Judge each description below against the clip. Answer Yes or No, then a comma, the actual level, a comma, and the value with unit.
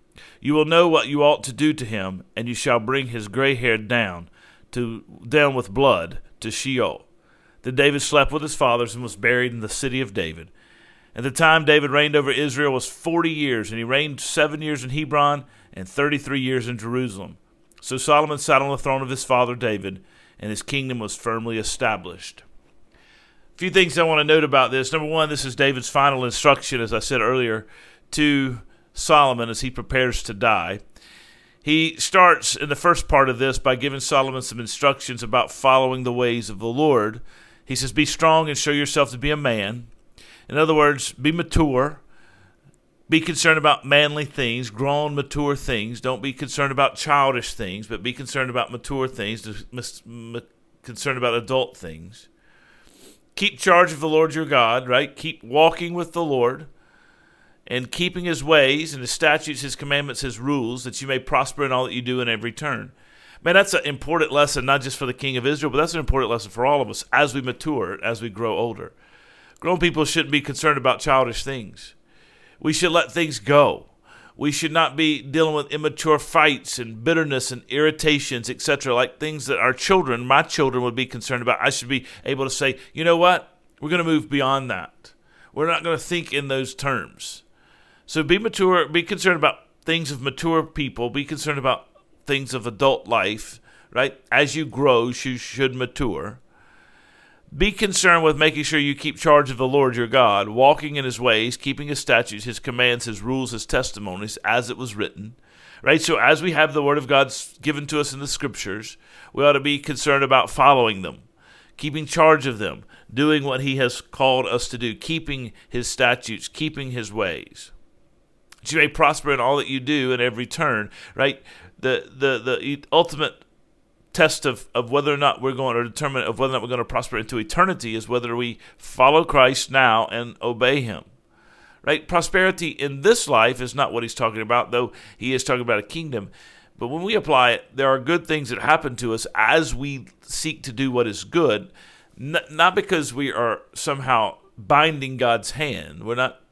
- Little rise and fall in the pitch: No, average, 3.5 semitones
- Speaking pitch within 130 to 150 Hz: Yes, low, 135 Hz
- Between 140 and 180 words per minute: No, average, 195 wpm